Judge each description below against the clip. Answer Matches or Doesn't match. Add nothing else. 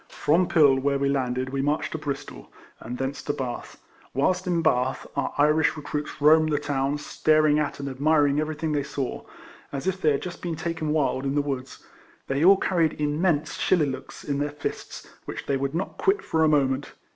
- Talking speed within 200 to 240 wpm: Matches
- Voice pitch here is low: Doesn't match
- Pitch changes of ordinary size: Doesn't match